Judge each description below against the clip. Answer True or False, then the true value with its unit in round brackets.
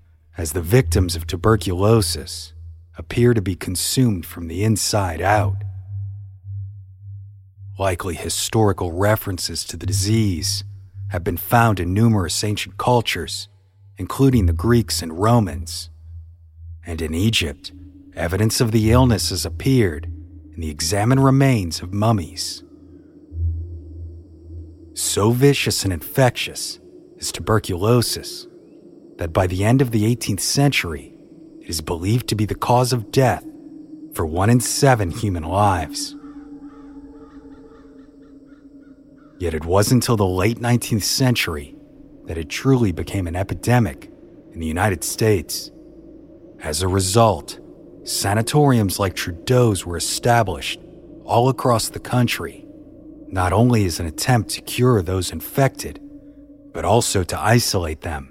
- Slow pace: True (120 wpm)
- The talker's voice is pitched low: True (100 Hz)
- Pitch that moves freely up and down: True (5.7 semitones)